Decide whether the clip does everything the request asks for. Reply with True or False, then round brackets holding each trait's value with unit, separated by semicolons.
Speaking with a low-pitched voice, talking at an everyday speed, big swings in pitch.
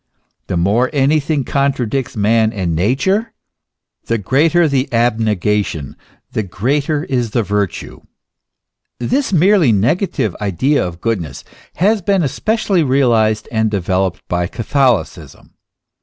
False (120 Hz; 110 wpm; 6.1 semitones)